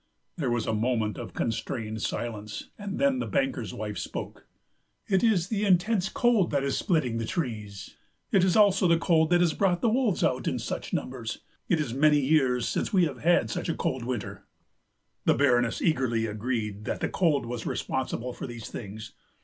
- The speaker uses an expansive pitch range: Yes, wide, 7.7 semitones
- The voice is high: No, medium, 140 Hz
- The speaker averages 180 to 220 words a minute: Yes, average, 190 wpm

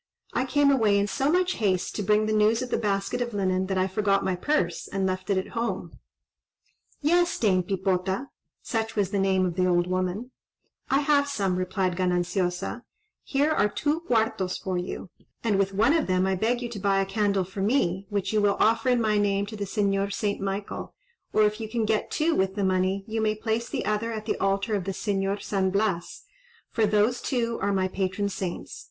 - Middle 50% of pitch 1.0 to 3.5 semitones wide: Yes, average, 3.0 semitones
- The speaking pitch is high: Yes, high, 200 Hz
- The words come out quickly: Yes, fast, 210 wpm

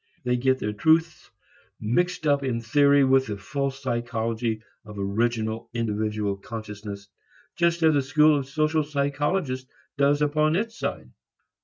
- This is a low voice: Yes, low, 130 Hz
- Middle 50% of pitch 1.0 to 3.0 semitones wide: No, average, 5.0 semitones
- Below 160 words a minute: Yes, average, 140 wpm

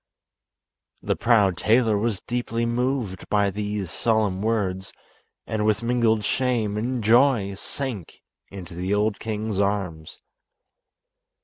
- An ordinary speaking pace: No, slow, 115 wpm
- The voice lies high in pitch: No, low, 105 Hz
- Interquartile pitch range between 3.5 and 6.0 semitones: No, average, 2.9 semitones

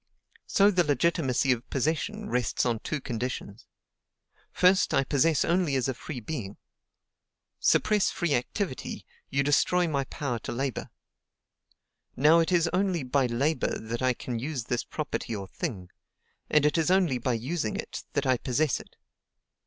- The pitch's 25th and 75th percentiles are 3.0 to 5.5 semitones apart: Yes, average, 5.2 semitones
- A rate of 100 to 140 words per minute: No, average, 155 wpm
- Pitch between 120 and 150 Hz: Yes, medium, 140 Hz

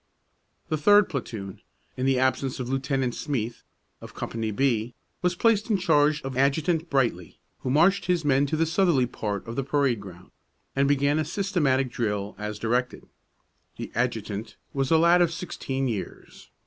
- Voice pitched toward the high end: No, low, 135 Hz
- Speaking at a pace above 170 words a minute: No, average, 165 wpm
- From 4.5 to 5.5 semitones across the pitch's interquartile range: Yes, average, 5.1 semitones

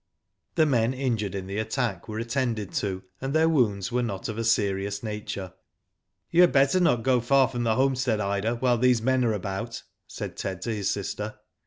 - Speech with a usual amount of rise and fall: Yes, average, 4.0 semitones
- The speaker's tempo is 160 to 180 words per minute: No, average, 195 wpm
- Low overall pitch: Yes, low, 115 Hz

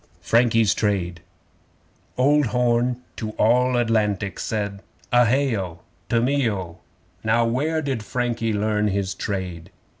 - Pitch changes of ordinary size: Yes, average, 3.5 semitones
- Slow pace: Yes, slow, 125 wpm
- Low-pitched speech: Yes, low, 115 Hz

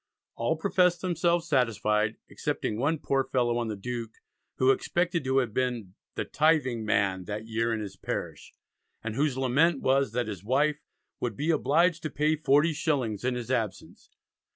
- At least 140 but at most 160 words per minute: No, average, 170 wpm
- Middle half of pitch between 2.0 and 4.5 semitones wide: No, wide, 5.4 semitones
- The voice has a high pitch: No, low, 130 Hz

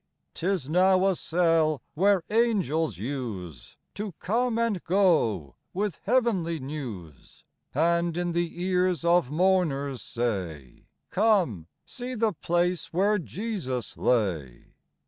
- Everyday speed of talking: No, slow, 115 wpm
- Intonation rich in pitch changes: Yes, wide, 7.0 semitones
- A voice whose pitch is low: No, medium, 170 Hz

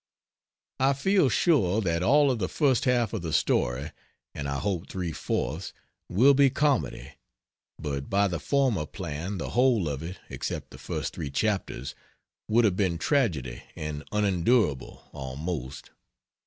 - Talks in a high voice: No, very low, 95 Hz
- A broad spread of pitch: Yes, wide, 8.5 semitones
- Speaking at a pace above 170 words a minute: No, average, 150 wpm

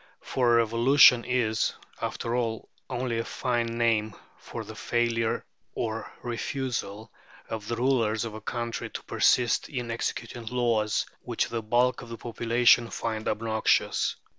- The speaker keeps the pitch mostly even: Yes, narrow, 1.4 semitones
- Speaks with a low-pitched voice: Yes, low, 115 Hz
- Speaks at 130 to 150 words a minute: Yes, average, 140 wpm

